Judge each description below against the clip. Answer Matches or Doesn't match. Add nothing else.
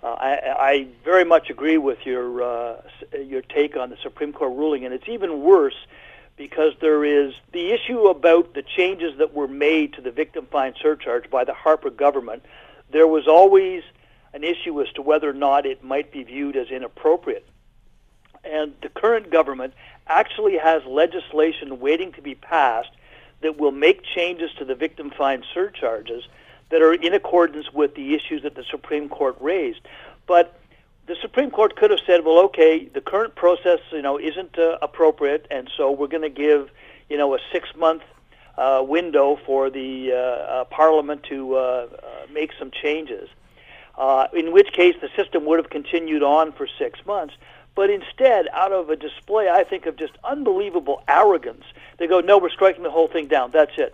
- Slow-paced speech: Doesn't match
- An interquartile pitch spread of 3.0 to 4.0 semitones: Doesn't match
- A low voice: Doesn't match